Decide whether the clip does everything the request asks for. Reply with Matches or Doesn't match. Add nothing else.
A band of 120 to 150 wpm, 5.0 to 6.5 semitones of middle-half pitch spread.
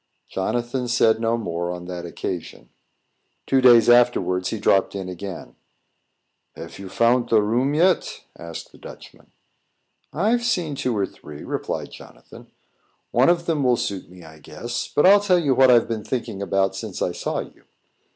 Doesn't match